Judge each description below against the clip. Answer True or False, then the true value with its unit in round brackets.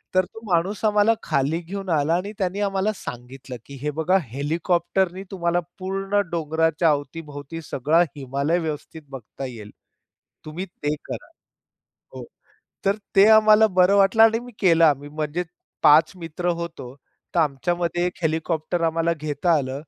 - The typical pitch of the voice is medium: True (165 Hz)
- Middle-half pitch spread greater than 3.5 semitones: True (4.0 semitones)